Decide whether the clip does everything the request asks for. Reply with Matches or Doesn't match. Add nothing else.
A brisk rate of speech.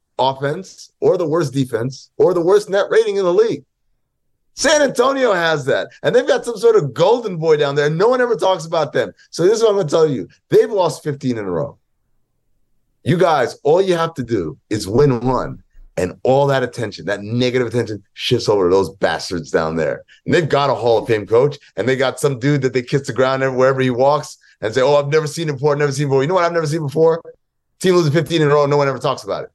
Matches